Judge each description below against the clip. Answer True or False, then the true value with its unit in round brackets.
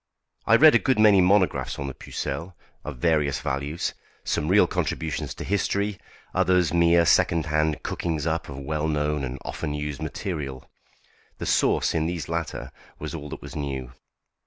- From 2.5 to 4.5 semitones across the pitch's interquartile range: True (3.2 semitones)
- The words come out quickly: False (165 wpm)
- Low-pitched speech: True (80 Hz)